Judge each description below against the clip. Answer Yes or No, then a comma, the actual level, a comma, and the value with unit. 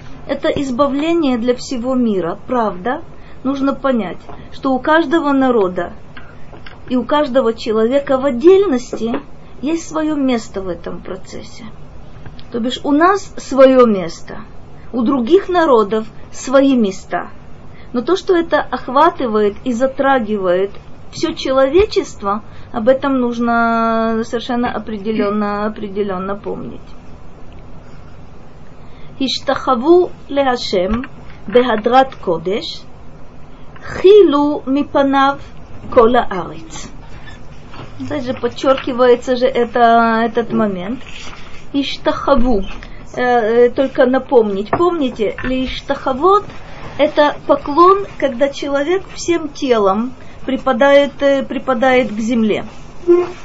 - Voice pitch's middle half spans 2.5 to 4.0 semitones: Yes, average, 3.6 semitones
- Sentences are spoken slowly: Yes, slow, 90 wpm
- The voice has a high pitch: Yes, very high, 265 Hz